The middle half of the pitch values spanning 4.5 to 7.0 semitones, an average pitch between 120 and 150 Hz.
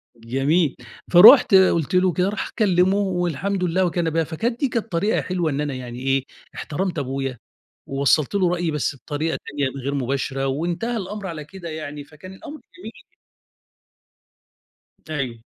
No: average, 5.2 semitones; medium, 165 Hz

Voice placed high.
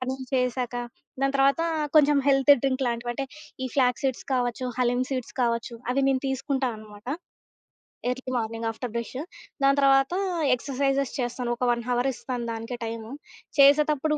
Yes: very high, 255 Hz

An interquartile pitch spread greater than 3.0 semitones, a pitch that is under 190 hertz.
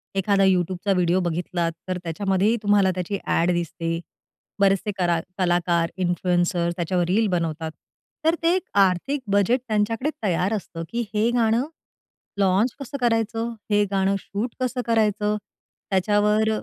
No: average, 3.6 semitones; high, 195 Hz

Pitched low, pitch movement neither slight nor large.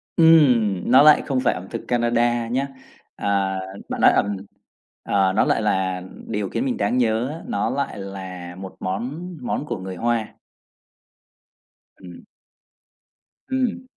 No: low, 115 Hz; wide, 6.0 semitones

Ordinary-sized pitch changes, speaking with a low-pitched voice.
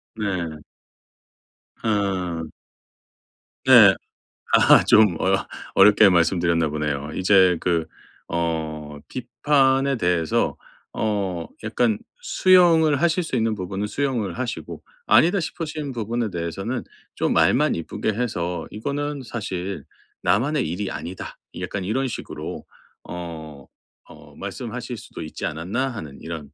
No: wide, 6.6 semitones; low, 100 Hz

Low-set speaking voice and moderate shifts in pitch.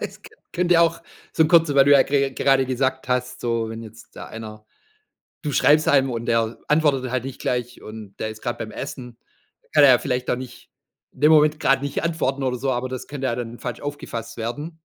Yes: low, 130 Hz; average, 3.4 semitones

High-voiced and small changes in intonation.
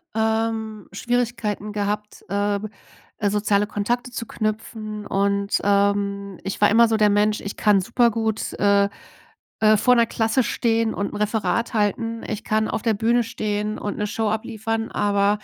Yes: high, 215 Hz; narrow, 1.7 semitones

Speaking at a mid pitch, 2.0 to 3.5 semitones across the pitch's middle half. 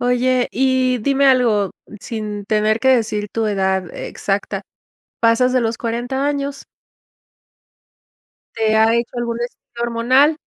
No: high, 235 Hz; average, 2.9 semitones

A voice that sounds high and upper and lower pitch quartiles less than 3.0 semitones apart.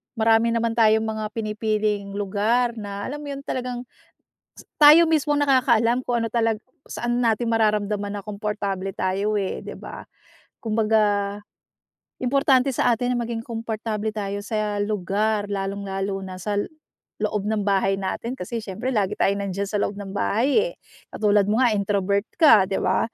Yes: high, 215 Hz; narrow, 2.6 semitones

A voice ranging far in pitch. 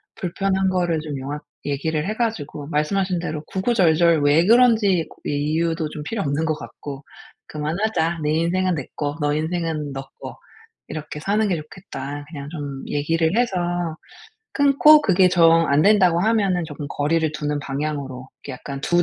No: average, 3.9 semitones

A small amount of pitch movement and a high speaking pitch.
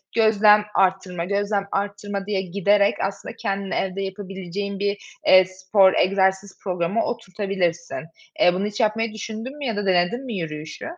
Yes: narrow, 1.8 semitones; high, 195 Hz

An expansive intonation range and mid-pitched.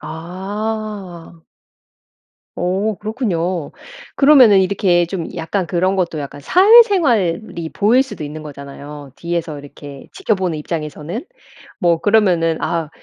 No: average, 4.8 semitones; medium, 175 Hz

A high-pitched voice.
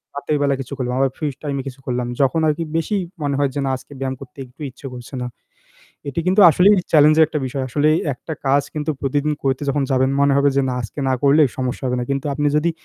No: medium, 140 Hz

